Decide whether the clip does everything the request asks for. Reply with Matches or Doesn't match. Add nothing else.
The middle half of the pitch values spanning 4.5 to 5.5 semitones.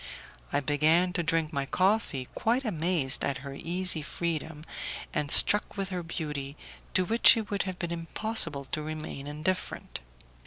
Doesn't match